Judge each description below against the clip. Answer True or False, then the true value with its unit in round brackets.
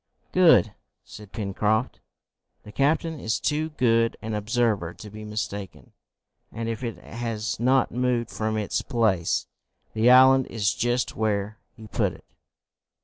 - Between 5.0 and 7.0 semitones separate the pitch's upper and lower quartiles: False (2.5 semitones)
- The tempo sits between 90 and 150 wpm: True (140 wpm)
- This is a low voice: True (110 Hz)